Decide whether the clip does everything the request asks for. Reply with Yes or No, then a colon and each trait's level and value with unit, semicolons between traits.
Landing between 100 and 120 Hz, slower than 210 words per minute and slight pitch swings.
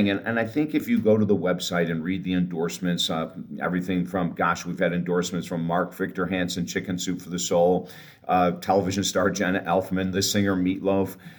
No: very low, 90 Hz; average, 200 wpm; narrow, 1.7 semitones